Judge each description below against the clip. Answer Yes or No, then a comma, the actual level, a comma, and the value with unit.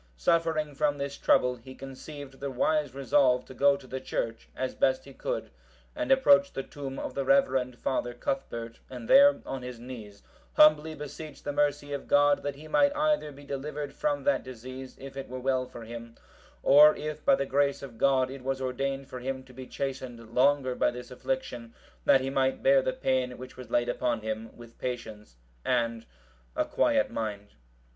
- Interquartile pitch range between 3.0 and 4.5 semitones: No, narrow, 2.4 semitones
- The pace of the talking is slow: No, average, 190 wpm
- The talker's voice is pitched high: No, low, 135 Hz